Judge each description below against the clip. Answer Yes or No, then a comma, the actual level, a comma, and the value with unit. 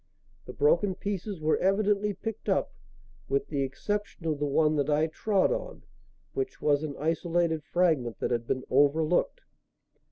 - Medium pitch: Yes, medium, 165 Hz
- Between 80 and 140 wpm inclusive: No, average, 155 wpm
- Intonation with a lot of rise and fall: Yes, wide, 5.8 semitones